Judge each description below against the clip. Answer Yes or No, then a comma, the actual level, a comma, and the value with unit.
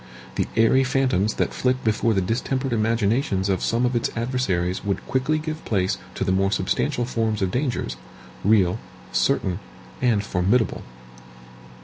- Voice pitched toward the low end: Yes, low, 115 Hz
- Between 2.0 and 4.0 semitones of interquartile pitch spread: No, average, 4.7 semitones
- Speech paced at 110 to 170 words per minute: Yes, average, 145 wpm